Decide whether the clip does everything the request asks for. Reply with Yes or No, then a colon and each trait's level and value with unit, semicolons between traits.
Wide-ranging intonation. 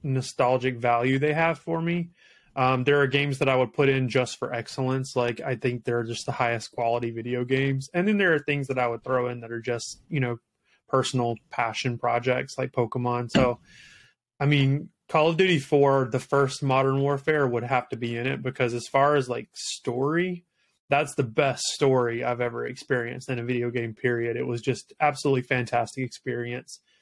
No: narrow, 2.6 semitones